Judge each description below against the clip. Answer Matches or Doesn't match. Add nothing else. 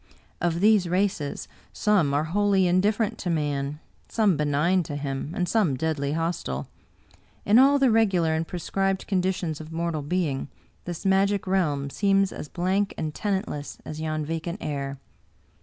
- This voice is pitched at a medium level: Matches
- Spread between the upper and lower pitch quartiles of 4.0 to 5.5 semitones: Matches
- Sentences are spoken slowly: Doesn't match